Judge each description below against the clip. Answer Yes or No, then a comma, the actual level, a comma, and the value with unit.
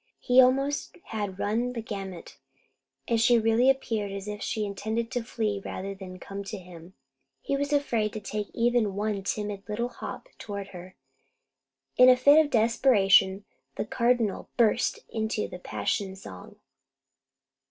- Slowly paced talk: No, average, 155 wpm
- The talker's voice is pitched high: Yes, high, 215 Hz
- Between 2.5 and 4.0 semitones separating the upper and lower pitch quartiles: Yes, average, 3.4 semitones